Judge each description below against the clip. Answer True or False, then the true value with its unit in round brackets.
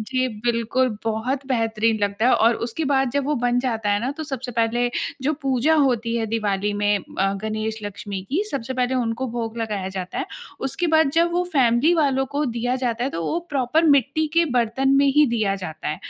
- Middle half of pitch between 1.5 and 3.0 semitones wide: False (3.5 semitones)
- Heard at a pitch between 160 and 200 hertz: False (240 Hz)